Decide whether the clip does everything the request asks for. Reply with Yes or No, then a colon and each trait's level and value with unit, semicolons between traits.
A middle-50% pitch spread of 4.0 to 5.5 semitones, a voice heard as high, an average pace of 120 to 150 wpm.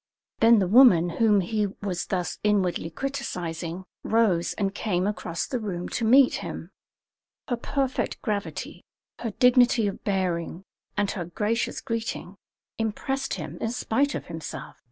Yes: average, 4.7 semitones; high, 210 Hz; average, 140 wpm